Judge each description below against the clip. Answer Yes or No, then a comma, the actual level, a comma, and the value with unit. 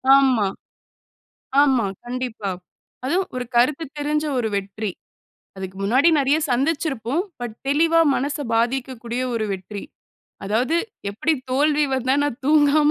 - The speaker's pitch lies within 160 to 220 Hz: No, very high, 260 Hz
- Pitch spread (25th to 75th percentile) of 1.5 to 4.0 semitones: No, average, 4.4 semitones